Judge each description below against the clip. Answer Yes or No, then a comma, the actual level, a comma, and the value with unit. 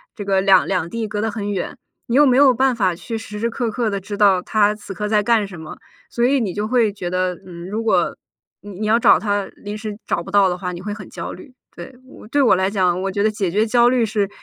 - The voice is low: No, high, 205 Hz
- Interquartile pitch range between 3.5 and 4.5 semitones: No, average, 2.9 semitones